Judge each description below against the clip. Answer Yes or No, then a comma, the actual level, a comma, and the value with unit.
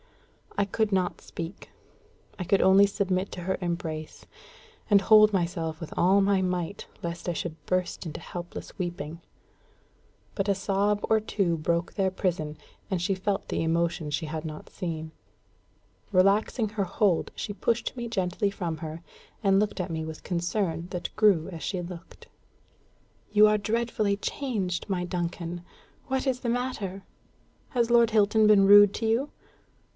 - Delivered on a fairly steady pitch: No, average, 3.3 semitones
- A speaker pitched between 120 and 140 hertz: No, high, 190 Hz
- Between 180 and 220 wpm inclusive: No, average, 160 wpm